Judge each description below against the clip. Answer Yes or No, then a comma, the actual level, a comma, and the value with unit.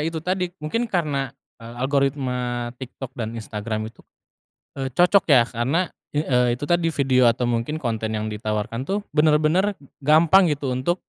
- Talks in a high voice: No, low, 135 Hz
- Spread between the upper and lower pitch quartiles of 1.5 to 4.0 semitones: No, average, 5.2 semitones